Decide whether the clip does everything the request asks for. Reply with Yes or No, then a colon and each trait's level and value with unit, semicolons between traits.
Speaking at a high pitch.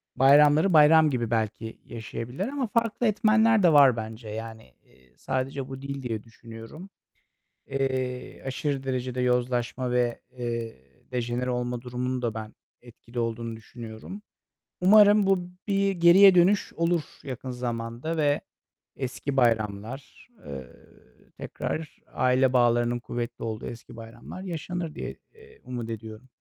No: low, 125 Hz